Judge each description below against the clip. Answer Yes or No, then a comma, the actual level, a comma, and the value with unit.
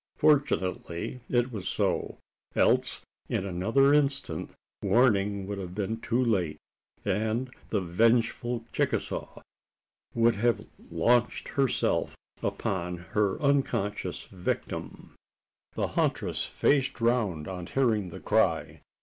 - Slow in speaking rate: Yes, slow, 105 wpm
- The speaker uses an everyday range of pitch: Yes, average, 4.5 semitones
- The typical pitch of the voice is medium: No, low, 110 Hz